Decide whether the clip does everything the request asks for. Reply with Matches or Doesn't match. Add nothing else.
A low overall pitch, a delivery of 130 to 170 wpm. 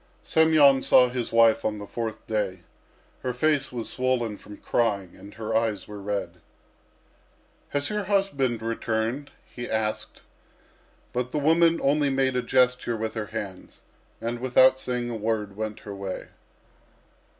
Matches